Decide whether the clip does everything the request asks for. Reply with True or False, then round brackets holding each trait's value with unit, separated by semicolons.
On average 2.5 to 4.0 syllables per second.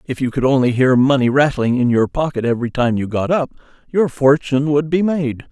False (5.7 syllables/s)